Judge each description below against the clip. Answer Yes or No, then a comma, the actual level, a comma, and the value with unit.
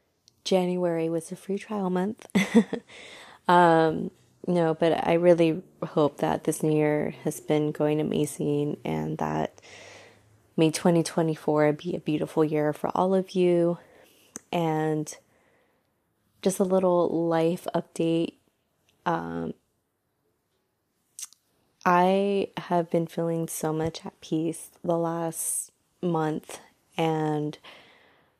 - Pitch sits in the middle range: Yes, medium, 165 Hz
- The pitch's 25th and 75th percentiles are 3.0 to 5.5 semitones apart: No, narrow, 2.6 semitones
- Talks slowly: Yes, slow, 110 wpm